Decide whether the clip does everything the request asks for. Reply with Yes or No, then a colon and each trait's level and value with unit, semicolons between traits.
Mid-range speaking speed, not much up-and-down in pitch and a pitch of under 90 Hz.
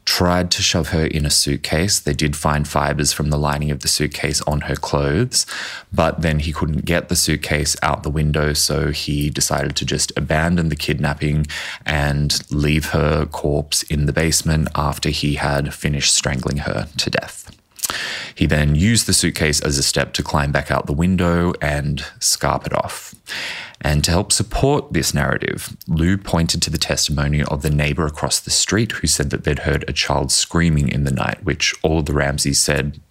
Yes: average, 190 wpm; narrow, 1.8 semitones; very low, 75 Hz